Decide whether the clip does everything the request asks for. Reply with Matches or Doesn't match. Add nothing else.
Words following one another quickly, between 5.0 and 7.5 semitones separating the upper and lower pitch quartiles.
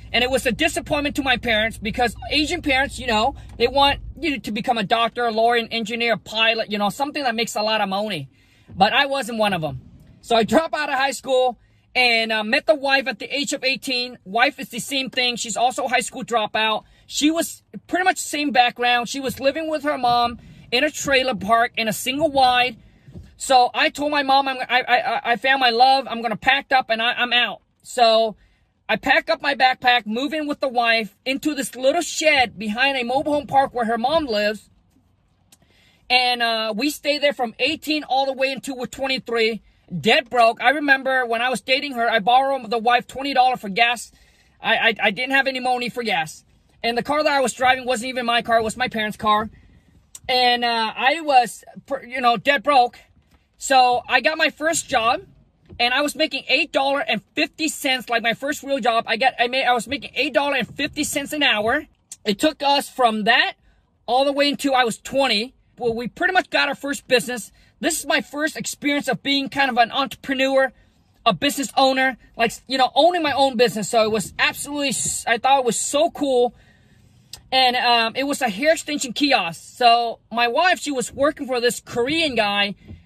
Doesn't match